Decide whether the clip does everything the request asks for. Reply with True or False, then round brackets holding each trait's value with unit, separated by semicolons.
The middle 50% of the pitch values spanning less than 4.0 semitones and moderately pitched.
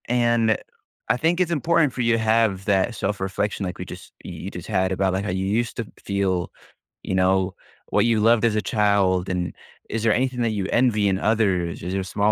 False (3.5 semitones; 105 Hz)